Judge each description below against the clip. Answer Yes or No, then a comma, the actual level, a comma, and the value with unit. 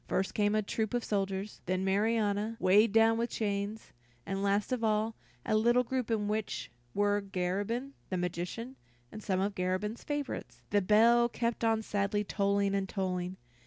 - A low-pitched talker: No, high, 210 Hz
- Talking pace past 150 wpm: Yes, average, 165 wpm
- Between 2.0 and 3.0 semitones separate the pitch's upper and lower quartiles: Yes, narrow, 2.4 semitones